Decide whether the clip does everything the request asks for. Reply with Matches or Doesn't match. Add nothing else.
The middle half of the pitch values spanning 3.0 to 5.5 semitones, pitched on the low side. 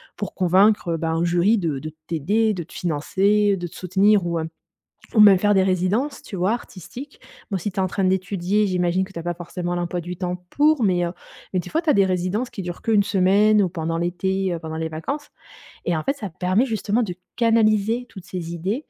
Doesn't match